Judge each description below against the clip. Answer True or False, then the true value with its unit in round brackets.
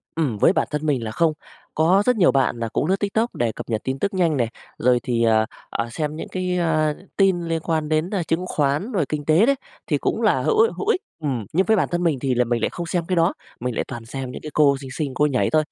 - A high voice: False (155 Hz)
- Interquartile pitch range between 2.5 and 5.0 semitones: False (5.4 semitones)